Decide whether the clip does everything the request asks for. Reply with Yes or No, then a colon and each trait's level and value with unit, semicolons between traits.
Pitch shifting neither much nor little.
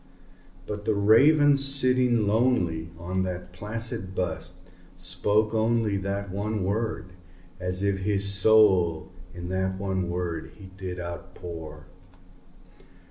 Yes: average, 3.4 semitones